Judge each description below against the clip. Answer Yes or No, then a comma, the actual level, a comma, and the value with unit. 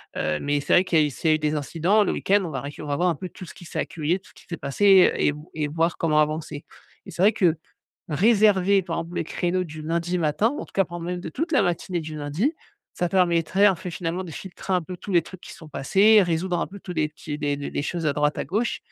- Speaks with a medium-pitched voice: Yes, medium, 170 Hz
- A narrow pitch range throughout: No, average, 3.5 semitones